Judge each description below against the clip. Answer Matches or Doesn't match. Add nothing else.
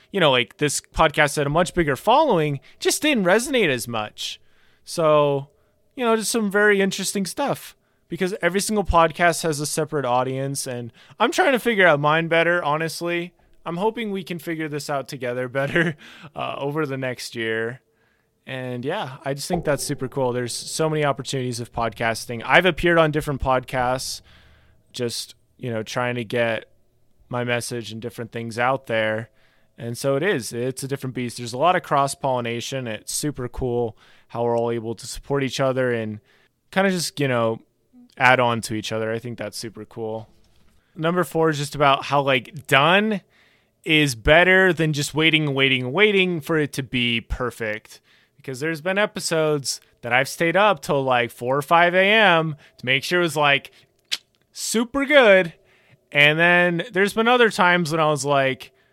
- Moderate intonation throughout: Doesn't match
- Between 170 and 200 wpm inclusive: Matches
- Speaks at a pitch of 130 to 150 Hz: Matches